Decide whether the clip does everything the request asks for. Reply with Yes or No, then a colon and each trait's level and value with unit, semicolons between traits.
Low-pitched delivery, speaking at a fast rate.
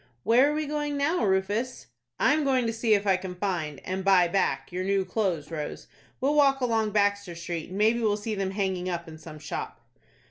No: high, 200 Hz; fast, 215 wpm